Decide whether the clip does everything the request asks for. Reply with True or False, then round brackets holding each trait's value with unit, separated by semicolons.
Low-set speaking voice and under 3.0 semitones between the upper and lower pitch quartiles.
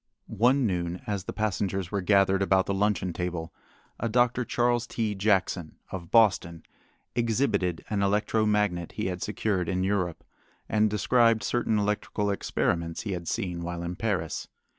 False (100 Hz; 3.4 semitones)